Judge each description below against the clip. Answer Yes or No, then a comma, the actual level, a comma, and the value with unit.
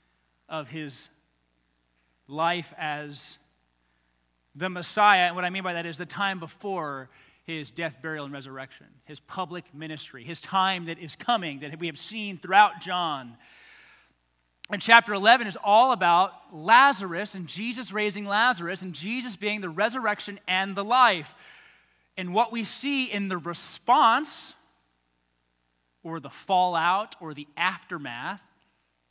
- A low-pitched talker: No, medium, 170 Hz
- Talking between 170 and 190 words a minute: No, average, 140 wpm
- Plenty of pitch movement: Yes, wide, 6.4 semitones